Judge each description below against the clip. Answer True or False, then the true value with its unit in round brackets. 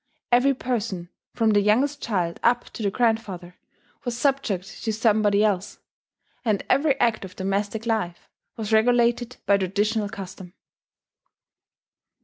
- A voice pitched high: True (215 Hz)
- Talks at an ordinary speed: False (125 wpm)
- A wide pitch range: False (3.4 semitones)